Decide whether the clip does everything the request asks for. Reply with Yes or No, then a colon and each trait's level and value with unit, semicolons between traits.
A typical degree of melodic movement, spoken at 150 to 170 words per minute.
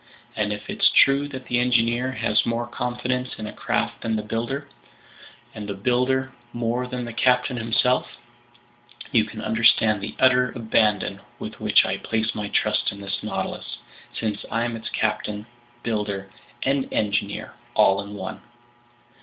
Yes: average, 3.0 semitones; average, 155 wpm